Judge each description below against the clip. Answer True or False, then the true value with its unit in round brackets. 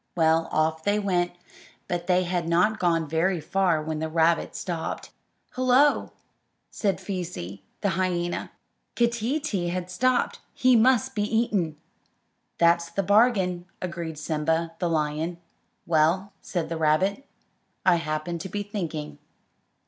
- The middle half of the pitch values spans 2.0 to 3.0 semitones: False (3.7 semitones)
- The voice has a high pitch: False (175 Hz)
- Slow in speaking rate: True (130 wpm)